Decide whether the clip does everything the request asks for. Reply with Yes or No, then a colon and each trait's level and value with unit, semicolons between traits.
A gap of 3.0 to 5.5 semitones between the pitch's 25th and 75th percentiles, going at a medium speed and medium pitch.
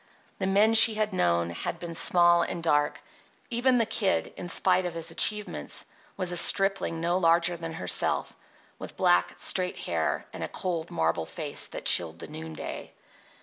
Yes: average, 3.4 semitones; average, 170 wpm; medium, 170 Hz